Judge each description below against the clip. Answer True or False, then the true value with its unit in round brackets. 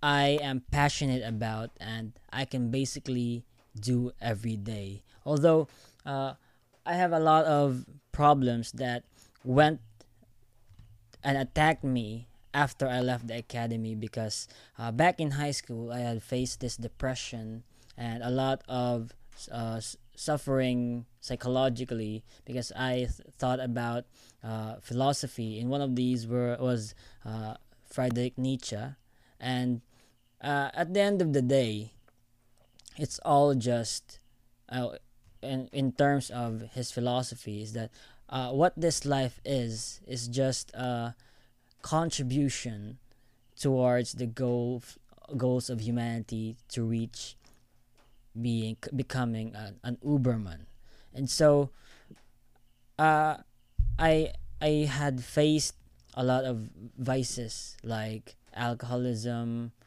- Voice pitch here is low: True (125 Hz)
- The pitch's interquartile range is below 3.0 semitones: True (2.4 semitones)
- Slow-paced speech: True (120 wpm)